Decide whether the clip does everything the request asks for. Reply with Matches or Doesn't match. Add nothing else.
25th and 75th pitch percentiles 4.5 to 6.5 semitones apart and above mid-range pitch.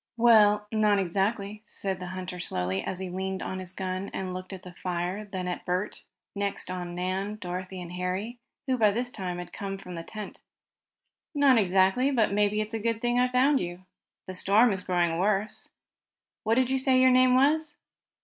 Doesn't match